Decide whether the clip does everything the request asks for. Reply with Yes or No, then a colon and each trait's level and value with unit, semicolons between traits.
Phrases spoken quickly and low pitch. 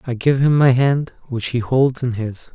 Yes: fast, 235 wpm; low, 125 Hz